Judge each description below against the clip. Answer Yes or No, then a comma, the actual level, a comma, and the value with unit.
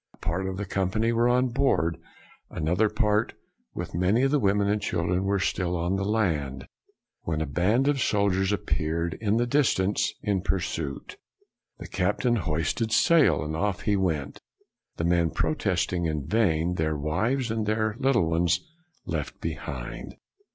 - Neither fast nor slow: Yes, average, 160 wpm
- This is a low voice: Yes, very low, 95 Hz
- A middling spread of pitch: Yes, average, 5.0 semitones